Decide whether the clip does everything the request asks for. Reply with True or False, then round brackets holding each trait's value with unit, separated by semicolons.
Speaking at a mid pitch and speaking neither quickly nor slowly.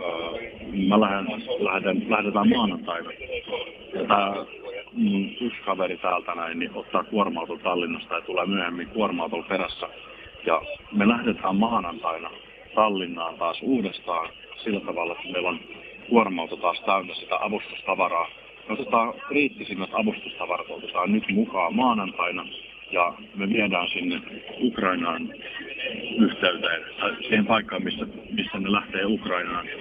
False (110 Hz; 115 wpm)